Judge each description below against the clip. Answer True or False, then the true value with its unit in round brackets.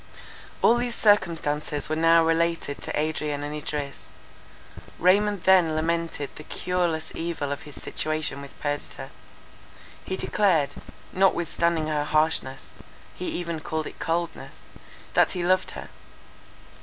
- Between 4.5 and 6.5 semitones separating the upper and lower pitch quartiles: False (2.8 semitones)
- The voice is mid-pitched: True (160 Hz)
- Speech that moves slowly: True (125 wpm)